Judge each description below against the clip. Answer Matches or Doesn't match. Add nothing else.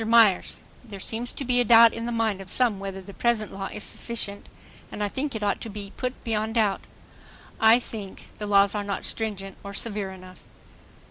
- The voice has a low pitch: Doesn't match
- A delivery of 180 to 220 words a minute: Matches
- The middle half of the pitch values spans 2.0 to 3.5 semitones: Matches